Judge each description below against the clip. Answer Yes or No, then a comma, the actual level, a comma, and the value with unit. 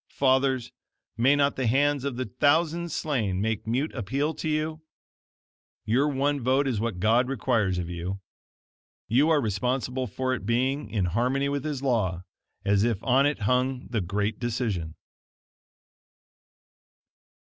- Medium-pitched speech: No, low, 125 Hz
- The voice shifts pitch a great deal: No, average, 4.5 semitones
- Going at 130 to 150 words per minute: Yes, average, 145 wpm